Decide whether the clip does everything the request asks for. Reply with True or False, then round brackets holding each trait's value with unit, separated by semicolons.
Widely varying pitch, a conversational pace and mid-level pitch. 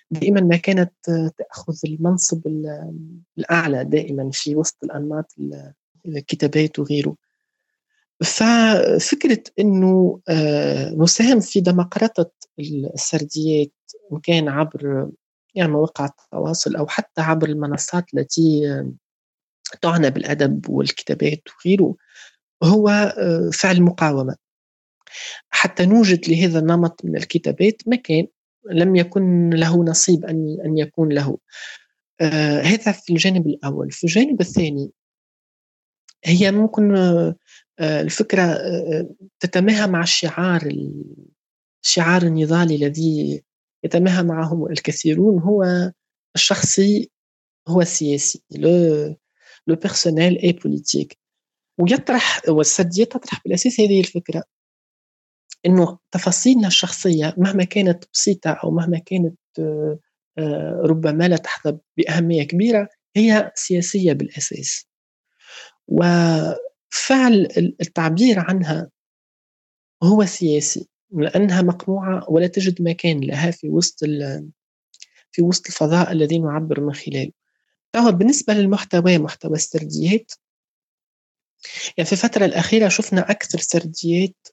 False (3.6 semitones; 95 wpm; 170 Hz)